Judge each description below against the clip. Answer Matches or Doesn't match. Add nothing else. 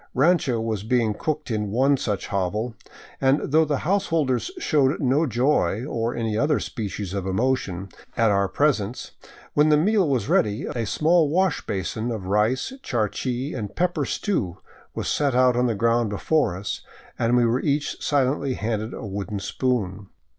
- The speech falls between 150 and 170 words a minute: Matches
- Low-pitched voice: Matches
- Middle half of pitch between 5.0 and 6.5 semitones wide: Matches